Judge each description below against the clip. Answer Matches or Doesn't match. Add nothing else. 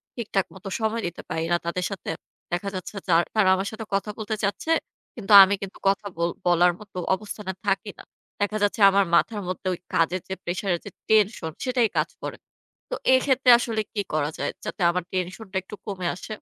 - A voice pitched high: Matches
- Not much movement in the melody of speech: Doesn't match